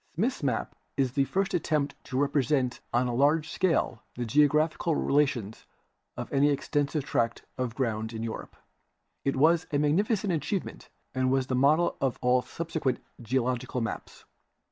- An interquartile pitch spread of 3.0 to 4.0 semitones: Yes, average, 3.6 semitones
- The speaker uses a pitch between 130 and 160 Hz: Yes, medium, 140 Hz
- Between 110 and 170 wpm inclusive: Yes, average, 150 wpm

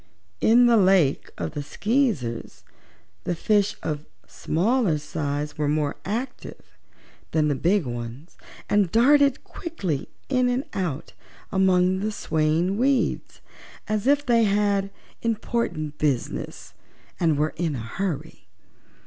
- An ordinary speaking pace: No, slow, 125 wpm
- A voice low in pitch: No, medium, 185 Hz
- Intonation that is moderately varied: No, wide, 6.9 semitones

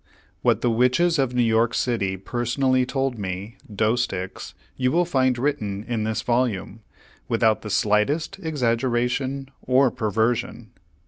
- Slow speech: Yes, slow, 130 wpm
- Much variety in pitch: No, average, 3.1 semitones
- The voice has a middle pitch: No, low, 120 Hz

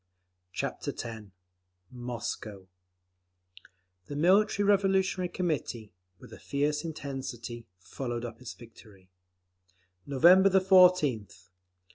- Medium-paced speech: No, slow, 85 wpm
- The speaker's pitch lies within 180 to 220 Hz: No, low, 135 Hz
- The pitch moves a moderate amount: No, wide, 8.0 semitones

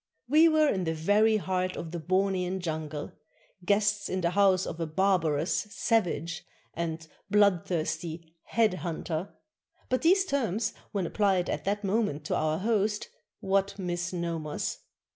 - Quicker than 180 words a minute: No, average, 145 wpm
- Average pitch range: Yes, average, 3.8 semitones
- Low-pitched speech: No, medium, 185 Hz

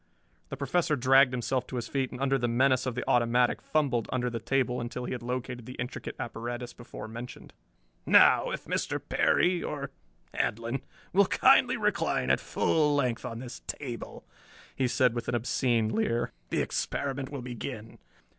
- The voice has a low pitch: Yes, low, 125 Hz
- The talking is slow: No, average, 170 wpm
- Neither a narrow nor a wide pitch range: No, narrow, 2.1 semitones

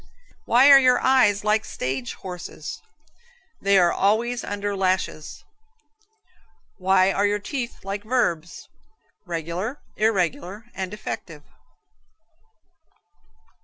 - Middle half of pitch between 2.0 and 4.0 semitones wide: Yes, average, 3.7 semitones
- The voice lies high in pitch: Yes, high, 200 Hz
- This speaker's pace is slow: Yes, slow, 95 wpm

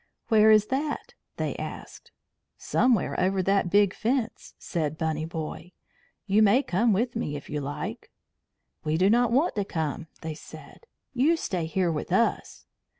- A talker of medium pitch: No, high, 195 Hz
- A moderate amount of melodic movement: No, wide, 6.3 semitones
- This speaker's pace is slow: No, average, 155 wpm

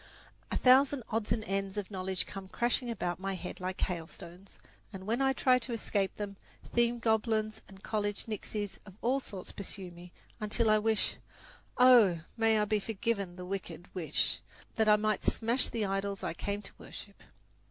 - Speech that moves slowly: No, average, 175 wpm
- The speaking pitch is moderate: No, high, 210 Hz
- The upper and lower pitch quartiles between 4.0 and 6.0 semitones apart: No, average, 2.9 semitones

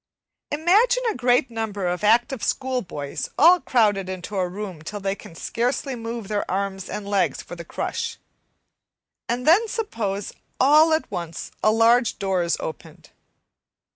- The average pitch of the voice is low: No, high, 215 Hz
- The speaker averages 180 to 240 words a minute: No, average, 150 wpm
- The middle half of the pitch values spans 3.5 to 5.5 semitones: Yes, average, 5.0 semitones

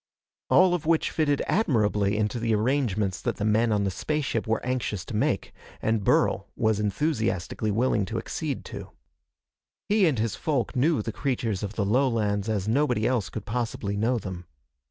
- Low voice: Yes, low, 110 Hz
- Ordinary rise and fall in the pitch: Yes, average, 4.0 semitones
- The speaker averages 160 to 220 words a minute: Yes, average, 175 wpm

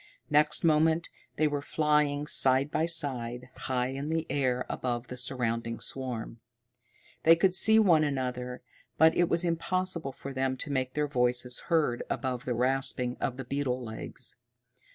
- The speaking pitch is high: No, low, 135 Hz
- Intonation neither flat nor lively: Yes, average, 3.7 semitones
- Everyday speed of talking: Yes, average, 155 wpm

